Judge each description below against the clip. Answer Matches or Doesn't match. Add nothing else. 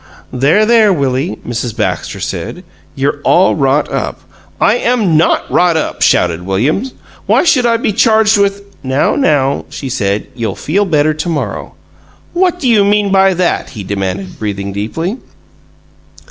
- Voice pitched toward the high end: Doesn't match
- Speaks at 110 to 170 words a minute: Matches